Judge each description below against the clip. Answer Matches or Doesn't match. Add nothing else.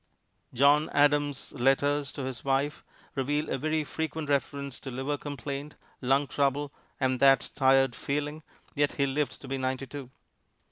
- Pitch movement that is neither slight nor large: Doesn't match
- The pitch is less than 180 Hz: Matches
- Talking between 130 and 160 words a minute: Matches